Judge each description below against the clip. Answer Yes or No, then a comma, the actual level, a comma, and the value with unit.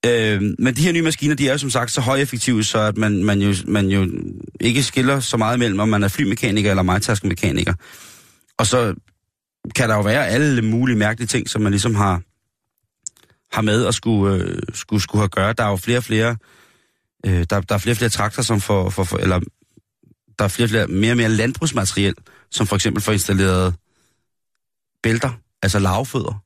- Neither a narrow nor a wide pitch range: Yes, average, 3.2 semitones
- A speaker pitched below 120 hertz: Yes, low, 110 Hz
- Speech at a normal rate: Yes, average, 195 wpm